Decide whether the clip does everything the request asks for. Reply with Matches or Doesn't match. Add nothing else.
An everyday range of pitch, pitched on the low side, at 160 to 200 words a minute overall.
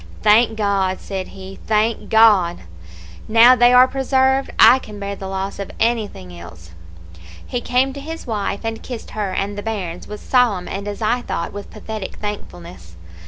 Doesn't match